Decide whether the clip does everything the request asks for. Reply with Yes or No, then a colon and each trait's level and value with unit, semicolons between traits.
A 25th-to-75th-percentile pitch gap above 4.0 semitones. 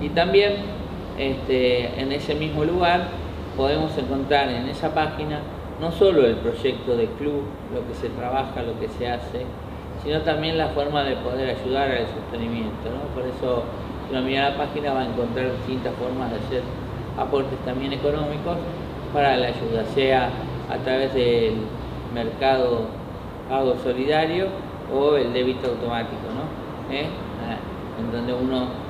No: average, 3.4 semitones